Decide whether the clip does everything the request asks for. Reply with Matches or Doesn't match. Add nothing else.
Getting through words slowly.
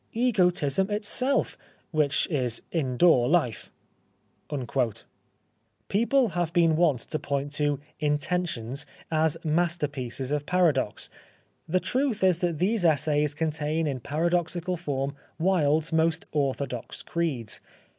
Matches